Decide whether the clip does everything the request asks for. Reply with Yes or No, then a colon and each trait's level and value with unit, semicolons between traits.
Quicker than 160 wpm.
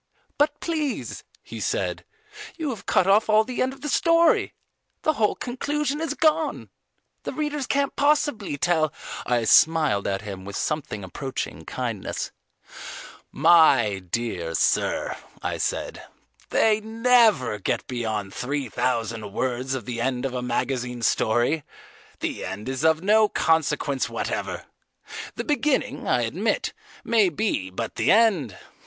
No: average, 140 wpm